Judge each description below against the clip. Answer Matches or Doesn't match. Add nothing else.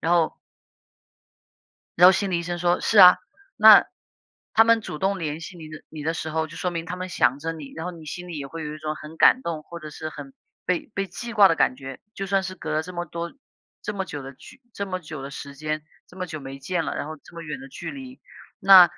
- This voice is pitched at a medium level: Matches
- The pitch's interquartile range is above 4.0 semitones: Doesn't match